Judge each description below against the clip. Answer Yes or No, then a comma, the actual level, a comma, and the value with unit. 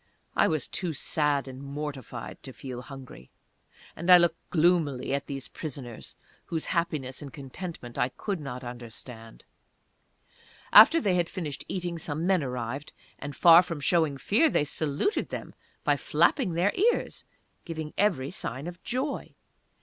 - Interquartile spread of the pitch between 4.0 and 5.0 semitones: Yes, average, 4.7 semitones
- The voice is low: No, medium, 150 Hz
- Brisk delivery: No, average, 150 wpm